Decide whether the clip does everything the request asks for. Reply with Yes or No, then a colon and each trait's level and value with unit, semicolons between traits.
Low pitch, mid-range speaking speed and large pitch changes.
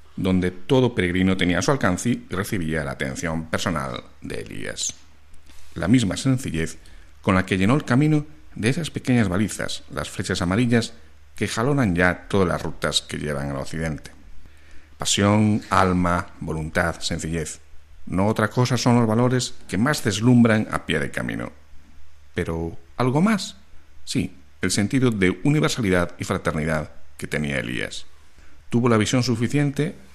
Yes: very low, 90 Hz; average, 145 wpm; wide, 7.1 semitones